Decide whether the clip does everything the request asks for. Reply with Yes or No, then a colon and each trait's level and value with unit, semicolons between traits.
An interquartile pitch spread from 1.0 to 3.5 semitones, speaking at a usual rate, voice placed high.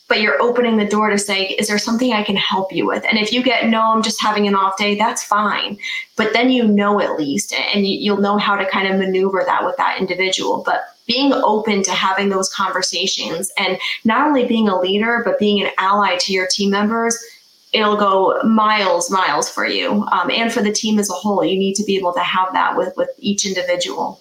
No: average, 2.7 semitones; fast, 235 wpm; high, 205 Hz